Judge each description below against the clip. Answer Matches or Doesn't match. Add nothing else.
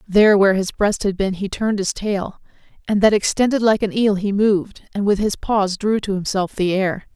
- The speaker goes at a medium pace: Doesn't match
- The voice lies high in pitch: Matches